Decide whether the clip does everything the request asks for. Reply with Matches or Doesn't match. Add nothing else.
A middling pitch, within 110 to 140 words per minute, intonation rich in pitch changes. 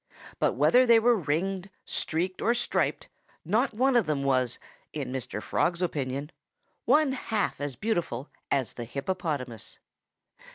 Matches